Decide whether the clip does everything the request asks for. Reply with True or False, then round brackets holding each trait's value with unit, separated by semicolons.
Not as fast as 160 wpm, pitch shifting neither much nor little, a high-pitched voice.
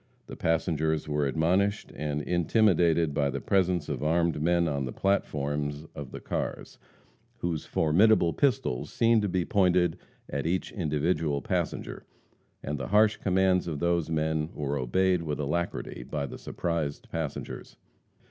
False (145 wpm; 3.6 semitones; 80 Hz)